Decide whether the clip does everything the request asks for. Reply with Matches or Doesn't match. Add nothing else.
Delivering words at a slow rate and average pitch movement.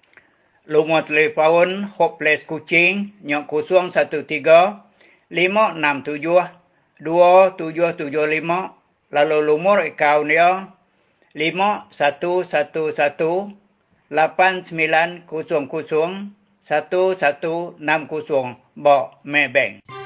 Matches